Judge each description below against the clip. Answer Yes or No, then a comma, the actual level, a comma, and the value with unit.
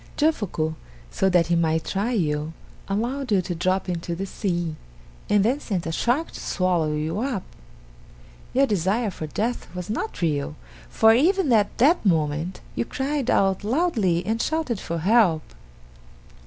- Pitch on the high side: Yes, high, 195 Hz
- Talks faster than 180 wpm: No, average, 155 wpm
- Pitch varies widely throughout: Yes, wide, 6.2 semitones